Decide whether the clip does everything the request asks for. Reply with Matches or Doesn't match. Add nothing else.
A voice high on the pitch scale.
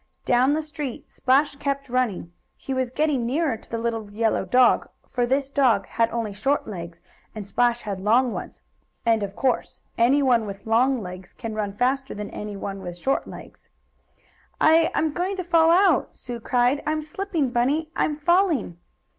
Matches